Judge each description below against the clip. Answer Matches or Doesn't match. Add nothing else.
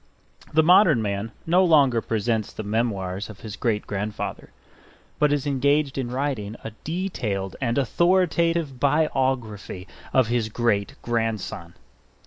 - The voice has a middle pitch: Doesn't match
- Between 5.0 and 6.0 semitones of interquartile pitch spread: Matches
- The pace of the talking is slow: Matches